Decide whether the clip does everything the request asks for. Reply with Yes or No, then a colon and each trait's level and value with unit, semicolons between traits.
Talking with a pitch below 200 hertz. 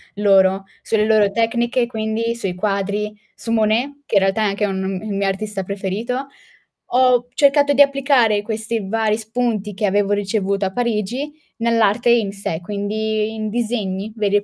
No: high, 215 Hz